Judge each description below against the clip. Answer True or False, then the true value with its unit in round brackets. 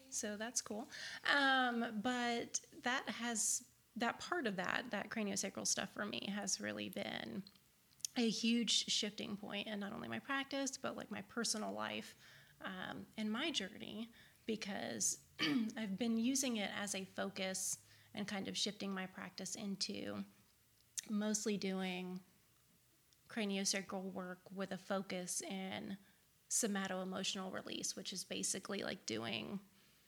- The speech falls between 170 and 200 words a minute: False (135 wpm)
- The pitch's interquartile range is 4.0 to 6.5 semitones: False (3.1 semitones)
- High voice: True (205 Hz)